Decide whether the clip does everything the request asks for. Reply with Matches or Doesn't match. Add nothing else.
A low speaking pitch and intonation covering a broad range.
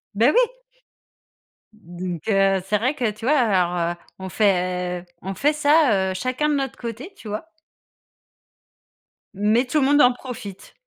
Doesn't match